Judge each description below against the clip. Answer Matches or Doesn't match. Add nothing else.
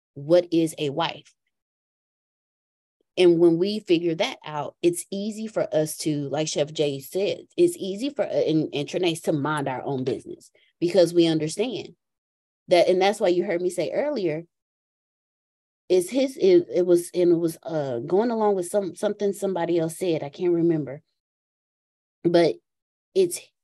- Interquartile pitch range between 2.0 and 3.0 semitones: Doesn't match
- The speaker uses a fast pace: Doesn't match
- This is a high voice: Doesn't match